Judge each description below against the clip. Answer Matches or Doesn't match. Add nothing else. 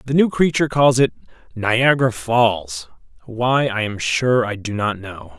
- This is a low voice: Matches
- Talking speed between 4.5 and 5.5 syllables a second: Doesn't match